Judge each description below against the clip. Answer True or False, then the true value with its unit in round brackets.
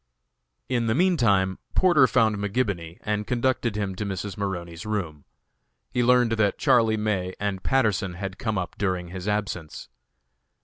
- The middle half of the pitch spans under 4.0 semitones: True (3.6 semitones)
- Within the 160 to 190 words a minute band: False (145 wpm)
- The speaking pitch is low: True (105 Hz)